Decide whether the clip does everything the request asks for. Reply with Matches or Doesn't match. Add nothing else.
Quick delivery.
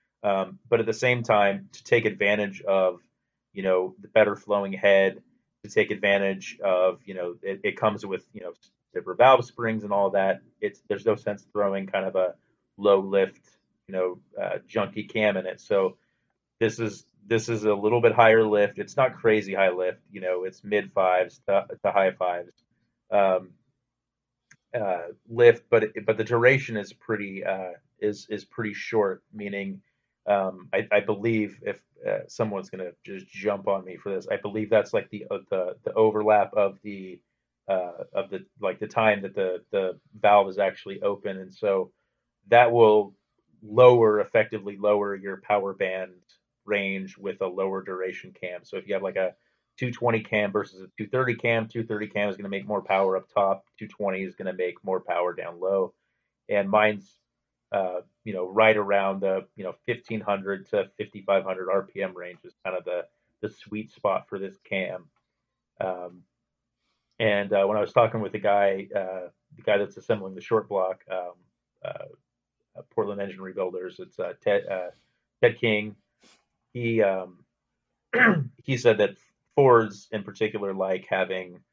Doesn't match